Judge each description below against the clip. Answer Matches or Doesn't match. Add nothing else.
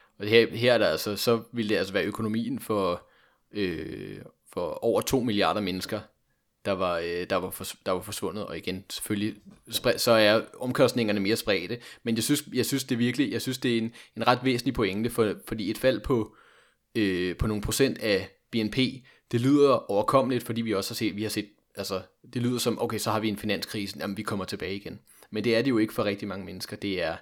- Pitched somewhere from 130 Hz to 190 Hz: Doesn't match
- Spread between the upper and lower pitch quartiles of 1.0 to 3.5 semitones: Matches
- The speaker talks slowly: Doesn't match